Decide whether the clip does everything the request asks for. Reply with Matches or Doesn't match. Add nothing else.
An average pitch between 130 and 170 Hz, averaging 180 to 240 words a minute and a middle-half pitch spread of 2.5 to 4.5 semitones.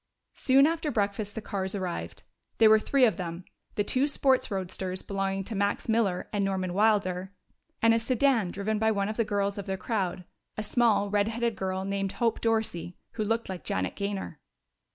Doesn't match